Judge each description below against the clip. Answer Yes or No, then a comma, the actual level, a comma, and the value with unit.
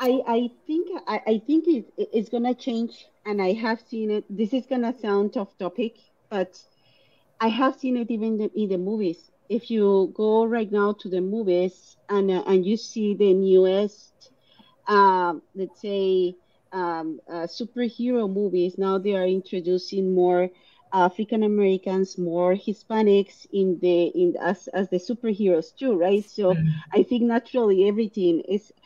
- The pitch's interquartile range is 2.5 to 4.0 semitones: Yes, average, 3.6 semitones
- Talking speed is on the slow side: No, average, 170 wpm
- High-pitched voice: Yes, high, 200 Hz